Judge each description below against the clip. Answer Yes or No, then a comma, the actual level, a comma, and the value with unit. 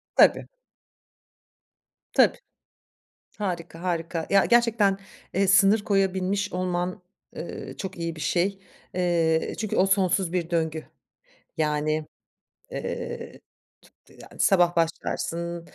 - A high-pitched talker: No, medium, 180 Hz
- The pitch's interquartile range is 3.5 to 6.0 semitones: No, average, 2.8 semitones